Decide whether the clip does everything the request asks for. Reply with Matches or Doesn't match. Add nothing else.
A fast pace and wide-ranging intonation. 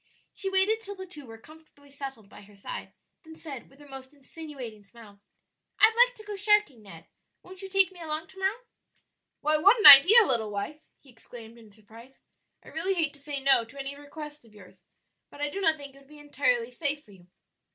Matches